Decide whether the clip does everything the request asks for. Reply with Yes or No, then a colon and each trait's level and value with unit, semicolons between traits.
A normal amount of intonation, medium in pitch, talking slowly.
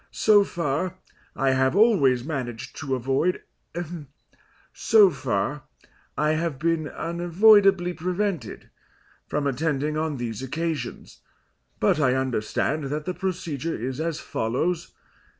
Yes: average, 4.7 semitones; medium, 155 Hz; slow, 115 wpm